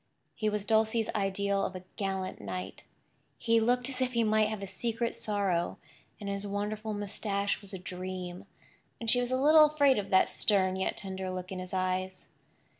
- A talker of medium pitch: No, high, 200 Hz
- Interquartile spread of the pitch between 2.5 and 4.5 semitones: Yes, average, 3.0 semitones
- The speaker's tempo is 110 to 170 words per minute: No, average, 190 wpm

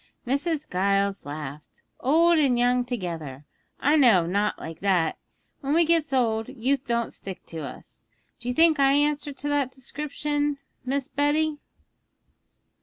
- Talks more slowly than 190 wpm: Yes, average, 150 wpm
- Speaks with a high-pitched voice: Yes, very high, 255 Hz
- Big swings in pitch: Yes, wide, 6.8 semitones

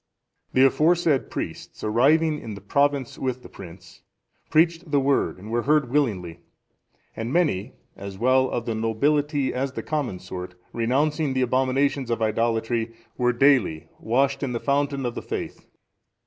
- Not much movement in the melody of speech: No, average, 4.1 semitones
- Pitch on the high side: No, low, 130 Hz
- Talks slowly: No, average, 160 wpm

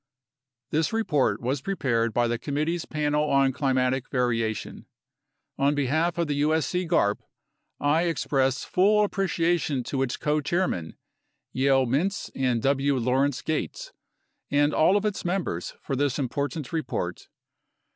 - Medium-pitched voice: Yes, medium, 145 Hz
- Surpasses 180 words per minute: No, slow, 135 wpm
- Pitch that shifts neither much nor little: Yes, average, 4.2 semitones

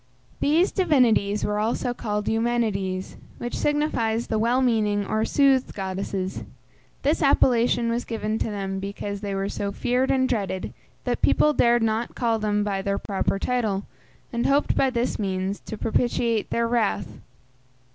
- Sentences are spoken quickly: No, average, 155 wpm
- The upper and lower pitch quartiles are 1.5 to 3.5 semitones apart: Yes, average, 3.2 semitones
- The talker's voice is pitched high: Yes, high, 225 Hz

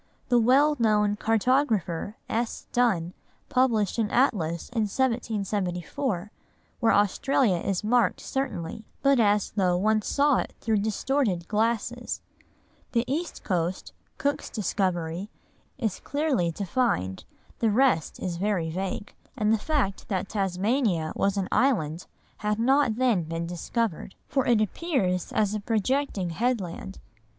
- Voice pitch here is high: Yes, high, 210 Hz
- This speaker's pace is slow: Yes, slow, 125 wpm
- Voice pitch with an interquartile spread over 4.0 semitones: Yes, average, 5.0 semitones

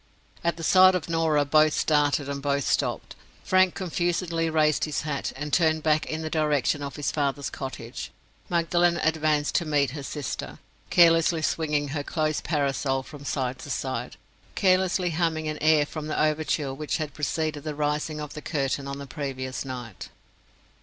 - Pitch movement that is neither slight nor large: No, narrow, 2.1 semitones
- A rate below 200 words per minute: Yes, average, 170 wpm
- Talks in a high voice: No, medium, 150 Hz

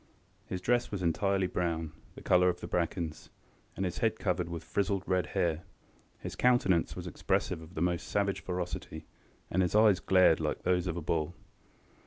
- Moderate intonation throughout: No, narrow, 2.3 semitones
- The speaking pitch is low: Yes, very low, 90 Hz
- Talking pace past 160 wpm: Yes, average, 180 wpm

